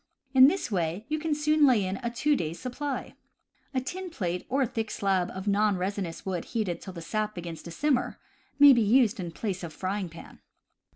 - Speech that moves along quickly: Yes, fast, 210 wpm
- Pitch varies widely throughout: Yes, wide, 6.4 semitones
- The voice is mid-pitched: No, high, 210 Hz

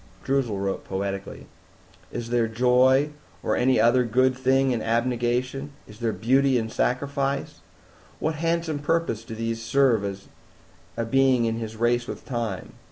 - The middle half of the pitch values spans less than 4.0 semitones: Yes, average, 3.0 semitones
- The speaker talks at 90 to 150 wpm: Yes, average, 145 wpm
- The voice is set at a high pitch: No, low, 120 Hz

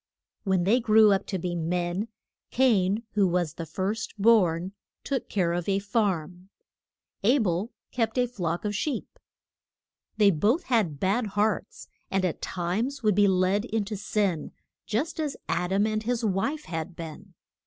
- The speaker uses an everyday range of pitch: Yes, average, 3.8 semitones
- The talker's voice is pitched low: No, high, 200 Hz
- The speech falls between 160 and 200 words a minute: Yes, average, 165 wpm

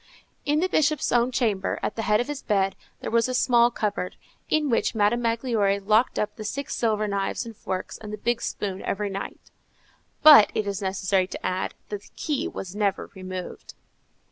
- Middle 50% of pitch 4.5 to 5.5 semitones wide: No, average, 3.5 semitones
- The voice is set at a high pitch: Yes, high, 215 Hz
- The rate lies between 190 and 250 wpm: Yes, average, 195 wpm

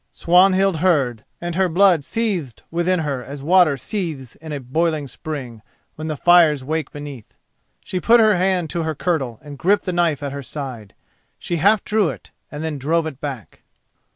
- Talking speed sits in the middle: Yes, average, 180 wpm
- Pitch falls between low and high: Yes, medium, 160 Hz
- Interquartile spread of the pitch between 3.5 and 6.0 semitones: Yes, average, 4.3 semitones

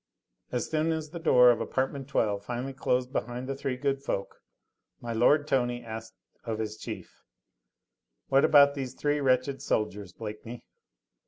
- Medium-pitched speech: No, low, 125 Hz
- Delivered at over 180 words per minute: No, average, 160 wpm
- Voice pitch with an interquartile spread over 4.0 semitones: No, average, 3.5 semitones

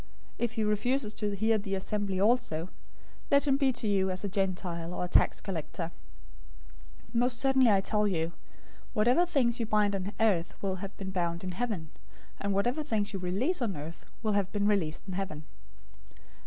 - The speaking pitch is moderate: No, high, 200 Hz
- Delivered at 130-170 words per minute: No, average, 185 wpm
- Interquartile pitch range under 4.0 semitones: Yes, average, 3.6 semitones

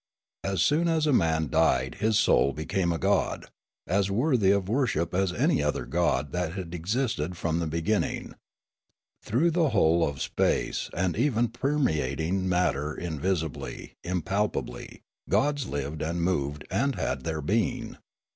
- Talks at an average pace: Yes, average, 145 wpm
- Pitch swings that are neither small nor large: No, wide, 6.0 semitones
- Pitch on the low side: Yes, very low, 90 Hz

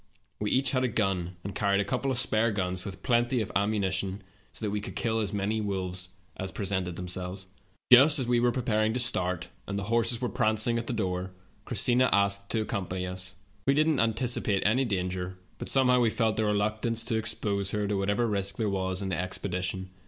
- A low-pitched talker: Yes, low, 105 Hz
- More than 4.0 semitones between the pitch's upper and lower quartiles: No, average, 3.7 semitones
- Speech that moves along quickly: Yes, fast, 215 wpm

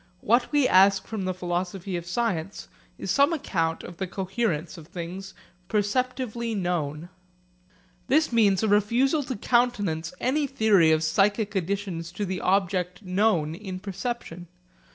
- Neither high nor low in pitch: No, high, 195 Hz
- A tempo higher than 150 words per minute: No, average, 140 wpm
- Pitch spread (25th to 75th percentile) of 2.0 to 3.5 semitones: No, average, 4.7 semitones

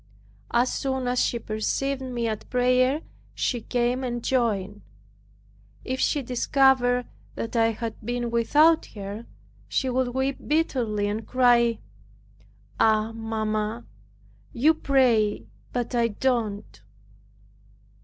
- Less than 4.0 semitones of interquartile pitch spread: Yes, average, 2.8 semitones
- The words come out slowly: Yes, slow, 115 wpm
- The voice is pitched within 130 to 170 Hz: No, high, 240 Hz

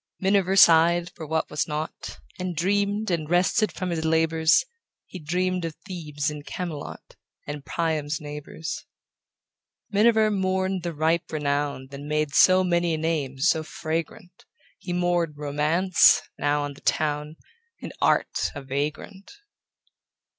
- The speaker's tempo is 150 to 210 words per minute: No, slow, 135 wpm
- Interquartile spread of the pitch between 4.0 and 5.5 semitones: No, average, 3.4 semitones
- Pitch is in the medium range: Yes, medium, 160 Hz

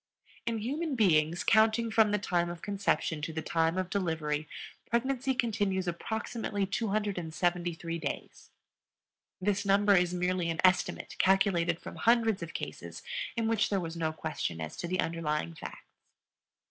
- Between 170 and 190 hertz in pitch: Yes, medium, 185 Hz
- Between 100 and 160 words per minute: Yes, average, 145 wpm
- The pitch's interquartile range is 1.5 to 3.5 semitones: No, average, 4.4 semitones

